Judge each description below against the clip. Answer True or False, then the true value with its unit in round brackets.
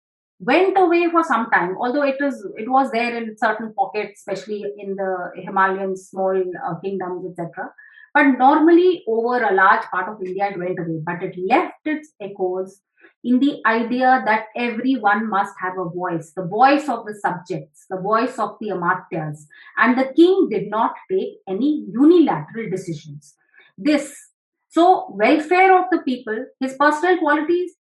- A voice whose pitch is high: True (220 Hz)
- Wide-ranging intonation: True (7.4 semitones)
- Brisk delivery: False (160 wpm)